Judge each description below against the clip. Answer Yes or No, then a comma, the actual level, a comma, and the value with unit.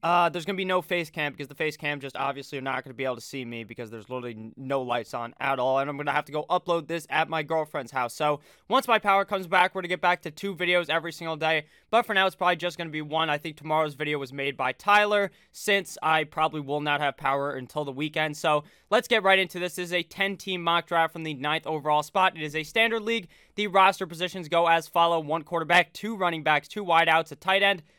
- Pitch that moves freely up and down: No, average, 3.7 semitones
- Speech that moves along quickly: Yes, fast, 265 wpm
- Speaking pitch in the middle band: Yes, medium, 160 Hz